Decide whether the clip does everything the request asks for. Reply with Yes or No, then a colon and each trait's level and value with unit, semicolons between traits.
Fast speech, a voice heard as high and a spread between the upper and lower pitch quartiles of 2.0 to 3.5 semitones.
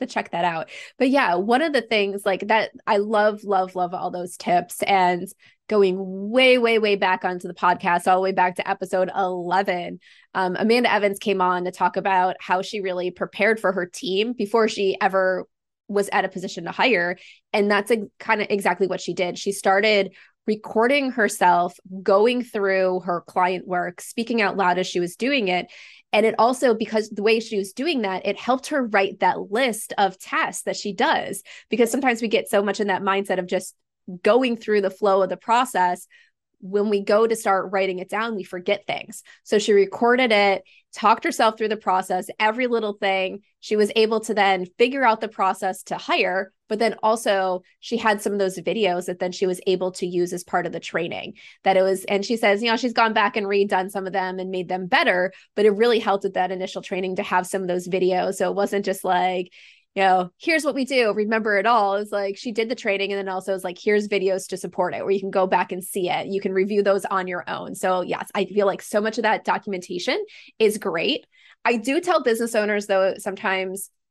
Yes: fast, 225 wpm; high, 195 Hz; average, 2.7 semitones